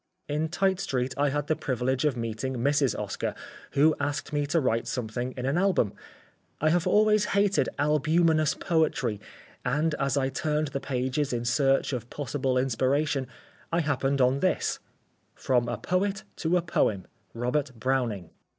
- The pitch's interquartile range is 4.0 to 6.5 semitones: No, average, 3.6 semitones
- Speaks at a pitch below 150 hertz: Yes, medium, 140 Hz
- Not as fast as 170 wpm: Yes, average, 160 wpm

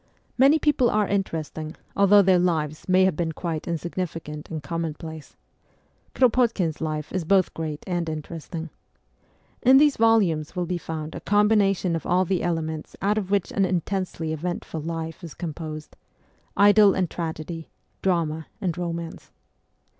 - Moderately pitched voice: Yes, medium, 170 Hz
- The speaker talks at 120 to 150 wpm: Yes, average, 145 wpm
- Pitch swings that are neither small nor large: Yes, average, 3.5 semitones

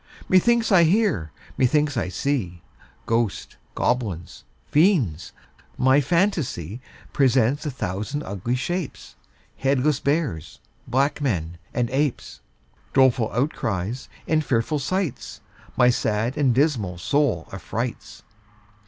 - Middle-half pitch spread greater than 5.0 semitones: Yes, wide, 5.4 semitones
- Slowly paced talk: Yes, slow, 105 wpm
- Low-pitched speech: Yes, low, 130 Hz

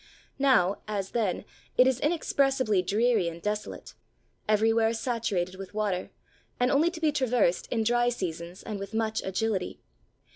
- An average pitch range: Yes, average, 4.3 semitones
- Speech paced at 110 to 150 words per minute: Yes, average, 145 wpm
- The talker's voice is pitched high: Yes, high, 220 Hz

